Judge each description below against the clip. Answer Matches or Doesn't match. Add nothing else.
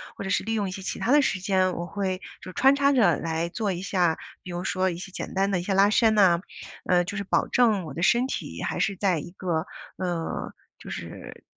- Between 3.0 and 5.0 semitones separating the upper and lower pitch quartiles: Doesn't match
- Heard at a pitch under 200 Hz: Matches